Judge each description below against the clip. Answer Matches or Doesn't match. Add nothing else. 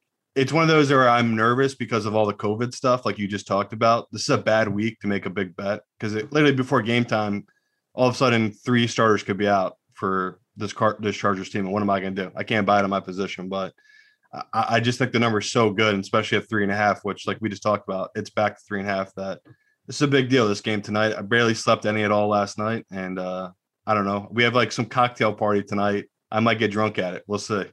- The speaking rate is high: Matches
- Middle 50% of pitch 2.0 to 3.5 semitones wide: Matches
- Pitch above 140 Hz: Doesn't match